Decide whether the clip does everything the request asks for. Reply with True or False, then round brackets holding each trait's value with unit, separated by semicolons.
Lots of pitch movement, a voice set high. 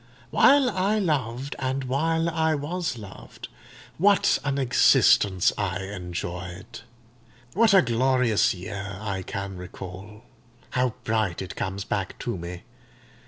False (7.1 semitones; 115 Hz)